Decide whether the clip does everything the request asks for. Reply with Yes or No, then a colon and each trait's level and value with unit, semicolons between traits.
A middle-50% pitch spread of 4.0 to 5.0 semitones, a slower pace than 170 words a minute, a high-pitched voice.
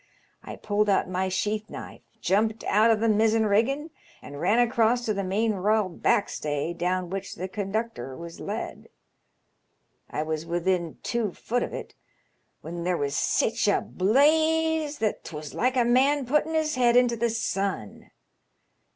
Yes: average, 4.7 semitones; average, 160 wpm; high, 215 Hz